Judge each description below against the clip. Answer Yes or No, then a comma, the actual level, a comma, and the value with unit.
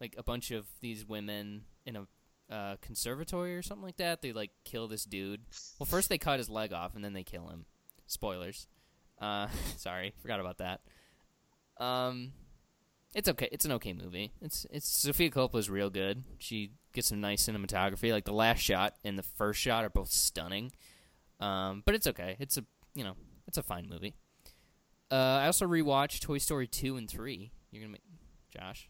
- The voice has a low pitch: Yes, low, 110 Hz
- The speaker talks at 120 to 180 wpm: No, average, 190 wpm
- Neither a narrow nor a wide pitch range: Yes, average, 5.0 semitones